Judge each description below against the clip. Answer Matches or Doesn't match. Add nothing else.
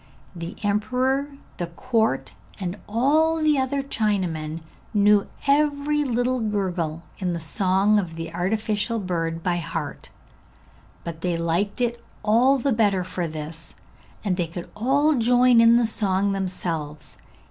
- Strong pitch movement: Matches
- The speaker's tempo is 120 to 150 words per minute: Matches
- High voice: Matches